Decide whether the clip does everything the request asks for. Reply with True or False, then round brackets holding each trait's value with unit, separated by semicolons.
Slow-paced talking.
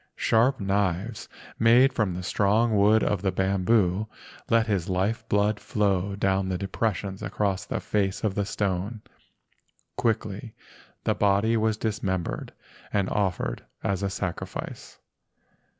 True (130 wpm)